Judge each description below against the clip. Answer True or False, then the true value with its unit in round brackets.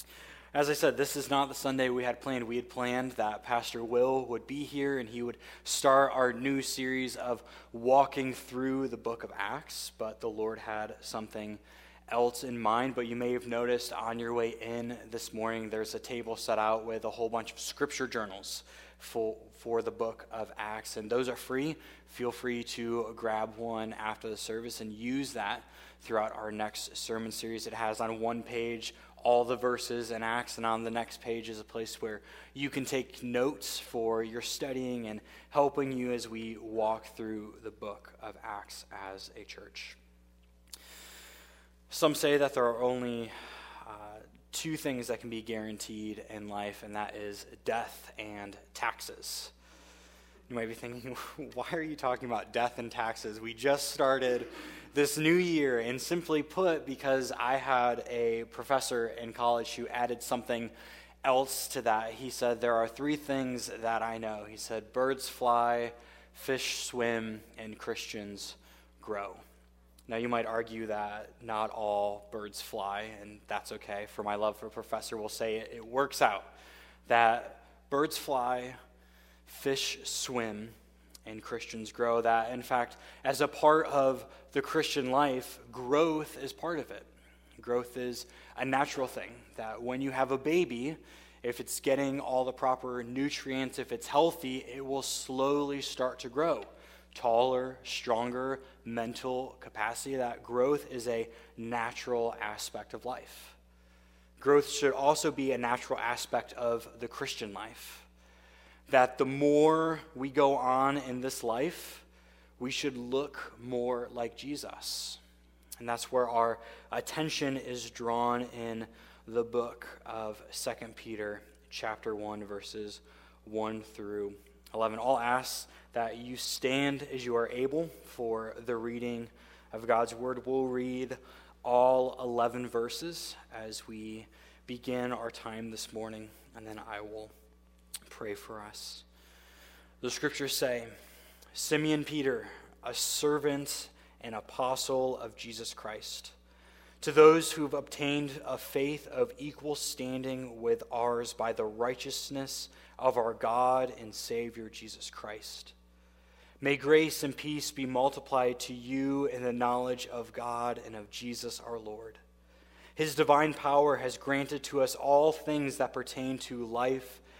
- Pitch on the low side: True (120 Hz)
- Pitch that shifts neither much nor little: True (3.3 semitones)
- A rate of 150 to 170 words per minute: True (155 wpm)